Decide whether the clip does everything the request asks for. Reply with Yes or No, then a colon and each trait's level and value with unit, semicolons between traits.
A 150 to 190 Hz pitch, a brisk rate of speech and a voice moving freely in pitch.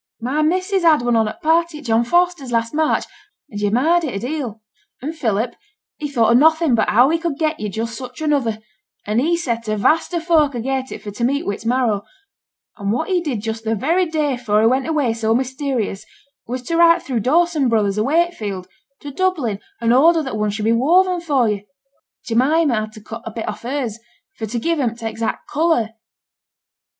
No: very high, 255 Hz; fast, 215 wpm; wide, 5.9 semitones